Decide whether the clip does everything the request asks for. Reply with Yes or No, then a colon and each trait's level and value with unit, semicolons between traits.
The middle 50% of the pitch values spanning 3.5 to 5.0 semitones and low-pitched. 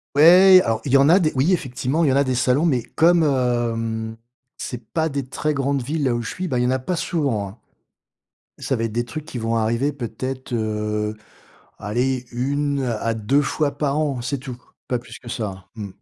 Yes: average, 4.0 semitones; low, 130 Hz